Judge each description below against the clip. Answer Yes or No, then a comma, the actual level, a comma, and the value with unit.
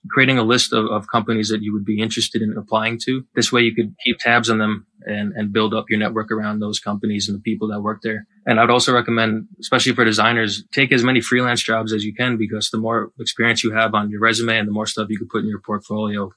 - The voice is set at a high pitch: No, low, 110 Hz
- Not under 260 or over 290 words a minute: Yes, fast, 265 wpm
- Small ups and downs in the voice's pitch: Yes, narrow, 1.6 semitones